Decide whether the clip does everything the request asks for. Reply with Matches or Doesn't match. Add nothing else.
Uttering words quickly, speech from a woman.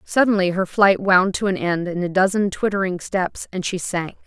Matches